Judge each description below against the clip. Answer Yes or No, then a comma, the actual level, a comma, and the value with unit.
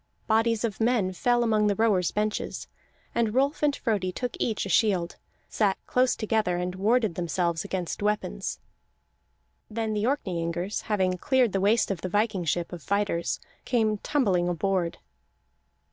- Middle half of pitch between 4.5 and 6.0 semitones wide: No, average, 3.9 semitones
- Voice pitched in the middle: No, high, 205 Hz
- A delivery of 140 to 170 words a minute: Yes, average, 150 wpm